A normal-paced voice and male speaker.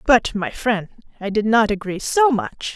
No: average, 195 wpm; female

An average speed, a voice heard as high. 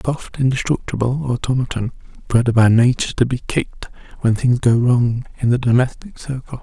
No: average, 165 wpm; low, 125 Hz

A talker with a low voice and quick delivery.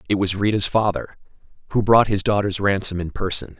No: low, 100 Hz; average, 185 wpm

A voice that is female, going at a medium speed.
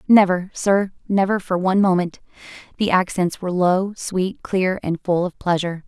Yes: female; average, 165 wpm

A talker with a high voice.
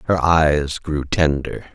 No: very low, 75 Hz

